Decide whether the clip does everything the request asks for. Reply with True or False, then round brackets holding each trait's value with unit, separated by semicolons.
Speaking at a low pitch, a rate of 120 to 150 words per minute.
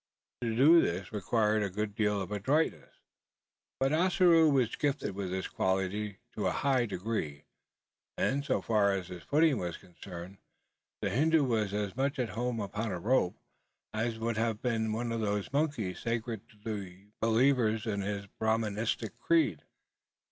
False (110 Hz; 160 wpm)